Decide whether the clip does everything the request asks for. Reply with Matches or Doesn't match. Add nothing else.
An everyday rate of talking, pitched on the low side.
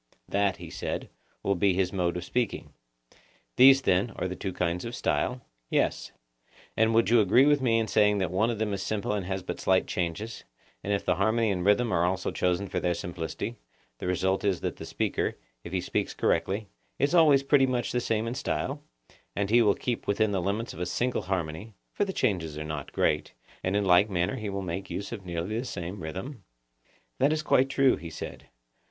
Doesn't match